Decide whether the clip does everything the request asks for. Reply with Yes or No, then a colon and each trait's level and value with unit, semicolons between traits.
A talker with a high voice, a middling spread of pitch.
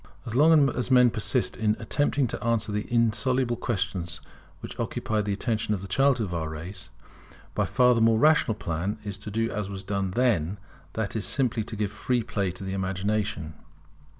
No: low, 110 Hz; average, 3.6 semitones